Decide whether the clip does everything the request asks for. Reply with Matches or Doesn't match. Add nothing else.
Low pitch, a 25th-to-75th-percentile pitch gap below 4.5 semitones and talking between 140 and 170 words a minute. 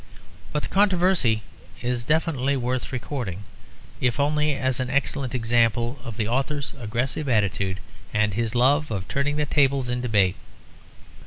Matches